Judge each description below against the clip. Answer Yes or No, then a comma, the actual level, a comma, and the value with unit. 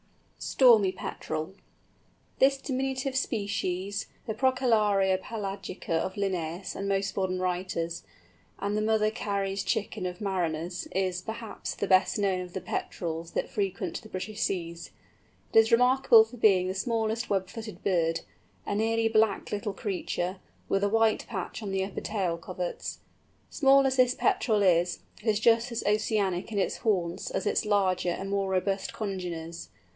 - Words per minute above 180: No, average, 155 wpm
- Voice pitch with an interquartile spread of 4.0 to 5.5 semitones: No, average, 3.2 semitones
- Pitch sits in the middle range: No, high, 200 Hz